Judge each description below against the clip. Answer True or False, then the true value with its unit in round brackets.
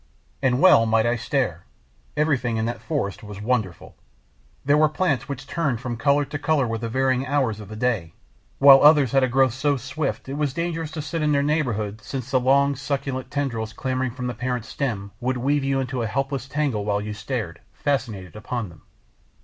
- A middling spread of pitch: True (4.0 semitones)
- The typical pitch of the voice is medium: False (130 Hz)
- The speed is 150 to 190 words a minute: False (200 wpm)